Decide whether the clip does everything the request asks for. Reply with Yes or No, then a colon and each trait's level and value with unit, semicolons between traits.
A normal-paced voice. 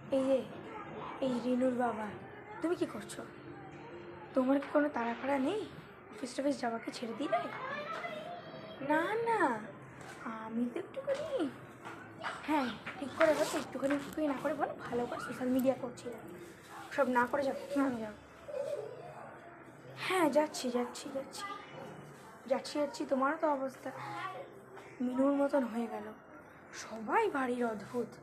No: fast, 125 wpm